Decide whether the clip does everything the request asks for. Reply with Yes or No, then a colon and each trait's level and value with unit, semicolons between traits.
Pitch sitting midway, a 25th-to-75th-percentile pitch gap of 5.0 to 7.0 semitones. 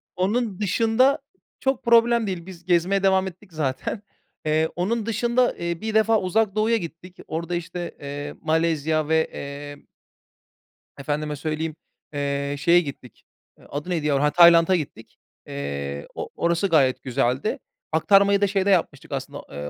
Yes: medium, 170 Hz; wide, 5.4 semitones